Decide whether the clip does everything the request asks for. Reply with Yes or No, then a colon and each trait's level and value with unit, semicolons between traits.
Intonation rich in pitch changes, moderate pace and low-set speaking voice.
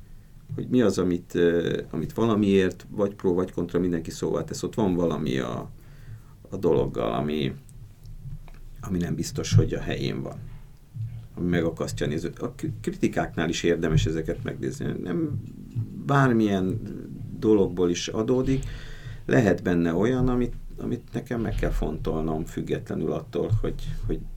Yes: wide, 6.4 semitones; average, 135 wpm; low, 110 Hz